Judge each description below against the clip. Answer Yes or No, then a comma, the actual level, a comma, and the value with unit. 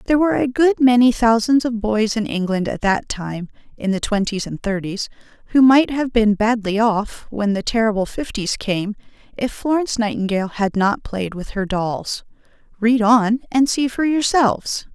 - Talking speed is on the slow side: No, average, 175 wpm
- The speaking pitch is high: Yes, high, 225 Hz